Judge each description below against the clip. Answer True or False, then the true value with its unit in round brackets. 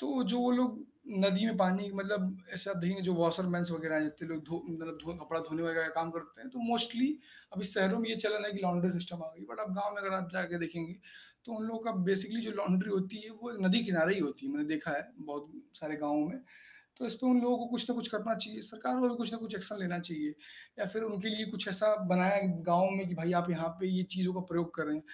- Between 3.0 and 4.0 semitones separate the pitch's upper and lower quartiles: False (4.6 semitones)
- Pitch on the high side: True (195 Hz)